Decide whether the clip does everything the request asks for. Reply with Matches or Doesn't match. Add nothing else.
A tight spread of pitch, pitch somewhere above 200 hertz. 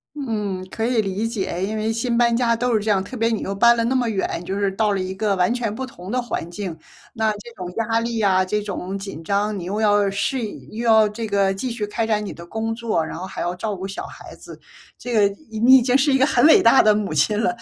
Doesn't match